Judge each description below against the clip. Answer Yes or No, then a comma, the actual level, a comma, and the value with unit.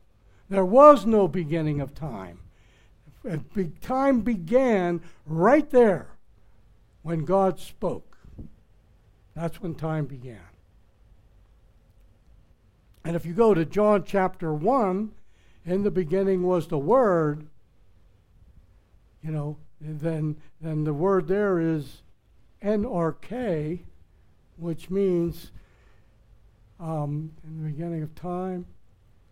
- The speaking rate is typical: No, slow, 105 wpm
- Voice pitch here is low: No, medium, 155 Hz